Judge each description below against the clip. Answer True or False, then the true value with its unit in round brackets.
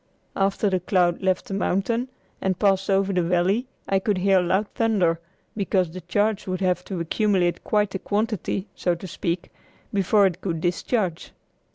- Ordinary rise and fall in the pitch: False (2.3 semitones)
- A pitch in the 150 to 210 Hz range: True (190 Hz)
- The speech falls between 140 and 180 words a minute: True (170 wpm)